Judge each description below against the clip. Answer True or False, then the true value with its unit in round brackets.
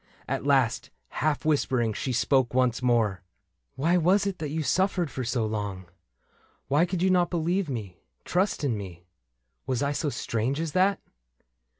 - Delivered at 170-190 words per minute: True (175 wpm)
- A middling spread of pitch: False (6.8 semitones)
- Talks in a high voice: False (140 Hz)